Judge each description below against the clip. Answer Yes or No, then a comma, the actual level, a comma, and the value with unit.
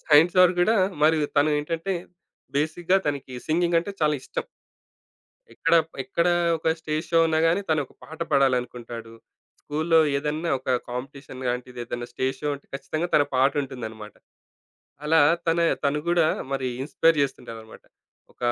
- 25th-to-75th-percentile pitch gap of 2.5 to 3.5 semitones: No, average, 4.0 semitones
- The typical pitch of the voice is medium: Yes, medium, 150 Hz